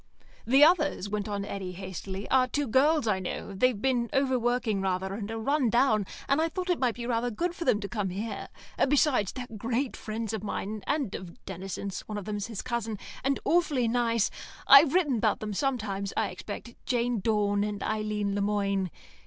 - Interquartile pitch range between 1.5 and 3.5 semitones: No, average, 4.3 semitones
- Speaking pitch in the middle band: No, high, 225 Hz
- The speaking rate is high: No, average, 195 wpm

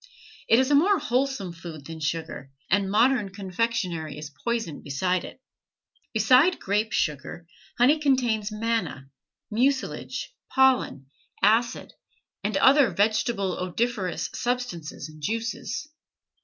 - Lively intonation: Yes, wide, 6.3 semitones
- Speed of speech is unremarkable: No, slow, 115 wpm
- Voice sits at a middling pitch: No, high, 215 Hz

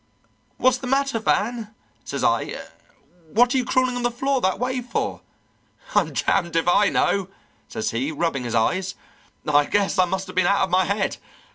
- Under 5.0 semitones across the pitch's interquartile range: No, average, 5.3 semitones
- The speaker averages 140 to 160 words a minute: No, average, 185 wpm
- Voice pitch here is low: No, high, 200 Hz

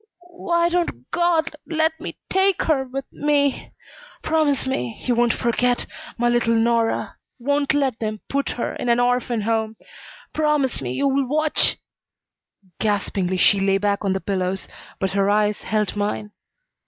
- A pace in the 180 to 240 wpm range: No, average, 155 wpm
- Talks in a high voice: Yes, high, 240 Hz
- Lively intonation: Yes, wide, 5.8 semitones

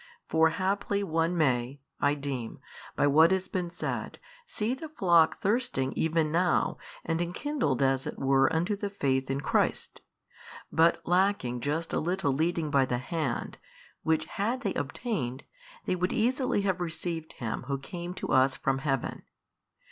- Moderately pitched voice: Yes, medium, 160 Hz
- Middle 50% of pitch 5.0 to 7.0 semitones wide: Yes, wide, 5.4 semitones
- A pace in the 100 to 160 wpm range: Yes, average, 155 wpm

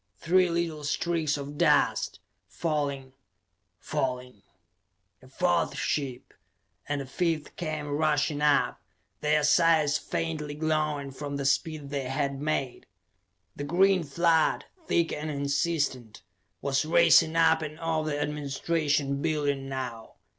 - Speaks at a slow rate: Yes, slow, 120 wpm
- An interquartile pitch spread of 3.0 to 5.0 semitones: No, narrow, 2.5 semitones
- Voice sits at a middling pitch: Yes, medium, 150 Hz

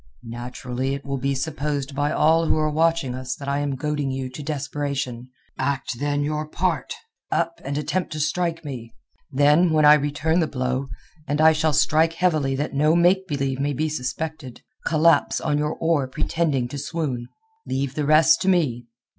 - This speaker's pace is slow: No, average, 175 wpm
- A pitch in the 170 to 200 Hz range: No, medium, 145 Hz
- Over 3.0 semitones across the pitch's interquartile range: No, average, 2.7 semitones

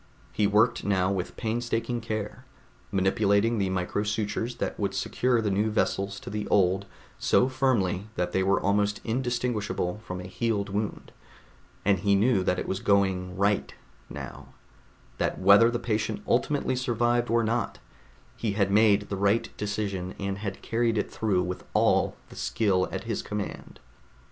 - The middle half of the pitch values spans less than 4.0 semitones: Yes, average, 2.8 semitones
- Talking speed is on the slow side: No, average, 160 wpm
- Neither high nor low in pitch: No, low, 105 Hz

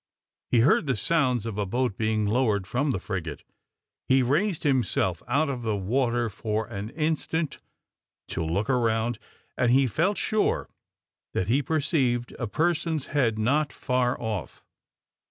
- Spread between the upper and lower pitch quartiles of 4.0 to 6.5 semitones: Yes, average, 4.6 semitones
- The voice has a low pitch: Yes, low, 120 Hz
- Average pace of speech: Yes, average, 150 wpm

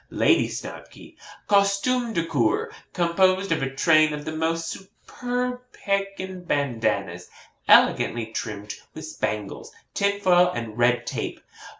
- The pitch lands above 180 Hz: No, medium, 165 Hz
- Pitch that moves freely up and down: Yes, wide, 8.6 semitones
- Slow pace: Yes, slow, 115 wpm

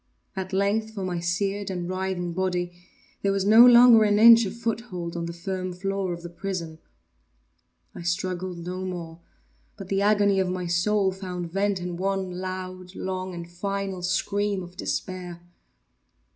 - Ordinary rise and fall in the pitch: No, narrow, 2.0 semitones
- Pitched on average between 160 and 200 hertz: Yes, medium, 185 Hz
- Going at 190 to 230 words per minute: No, average, 160 wpm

